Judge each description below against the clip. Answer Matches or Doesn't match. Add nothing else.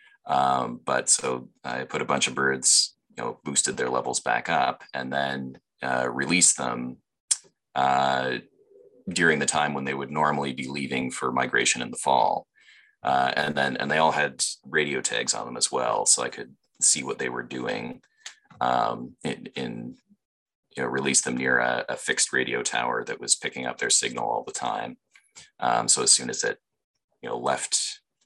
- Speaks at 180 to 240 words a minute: Matches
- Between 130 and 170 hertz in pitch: Doesn't match